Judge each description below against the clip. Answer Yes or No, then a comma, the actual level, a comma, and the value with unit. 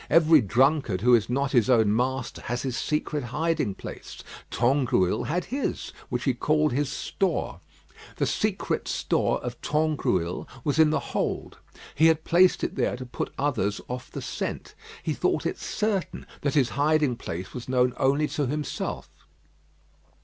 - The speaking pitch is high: No, low, 135 Hz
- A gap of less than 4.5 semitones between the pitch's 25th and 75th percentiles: Yes, average, 3.9 semitones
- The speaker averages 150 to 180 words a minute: Yes, average, 160 wpm